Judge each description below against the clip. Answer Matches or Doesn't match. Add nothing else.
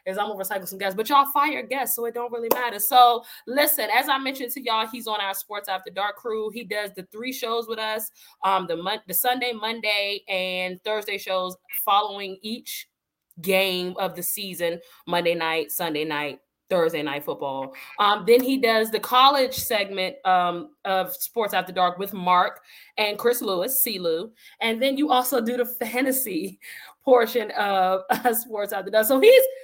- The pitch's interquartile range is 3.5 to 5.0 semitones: Matches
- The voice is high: Matches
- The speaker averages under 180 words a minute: Doesn't match